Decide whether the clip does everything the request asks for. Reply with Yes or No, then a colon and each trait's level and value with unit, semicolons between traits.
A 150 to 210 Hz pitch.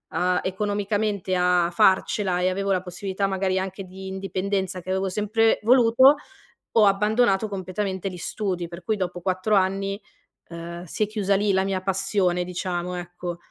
Yes: high, 190 Hz